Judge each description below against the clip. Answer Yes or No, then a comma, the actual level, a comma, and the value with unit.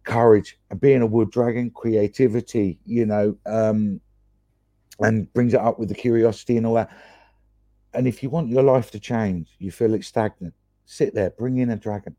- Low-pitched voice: Yes, low, 110 Hz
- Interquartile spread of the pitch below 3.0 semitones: Yes, narrow, 2.6 semitones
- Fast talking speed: No, average, 185 wpm